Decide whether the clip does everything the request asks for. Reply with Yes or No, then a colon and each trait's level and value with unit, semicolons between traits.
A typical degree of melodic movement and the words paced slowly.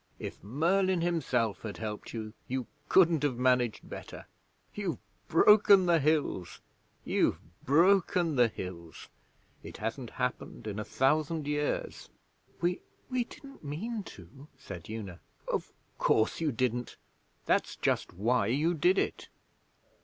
No: wide, 7.3 semitones; slow, 130 wpm